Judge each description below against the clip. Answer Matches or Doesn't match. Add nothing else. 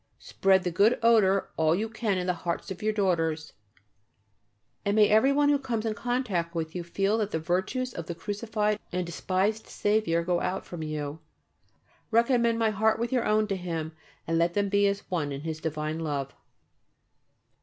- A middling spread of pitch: Matches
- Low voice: Doesn't match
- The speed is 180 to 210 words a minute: Matches